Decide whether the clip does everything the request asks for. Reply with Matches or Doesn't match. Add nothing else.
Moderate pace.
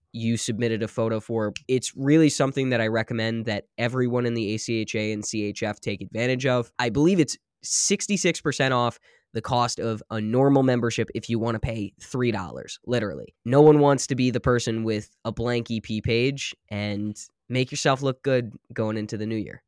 Matches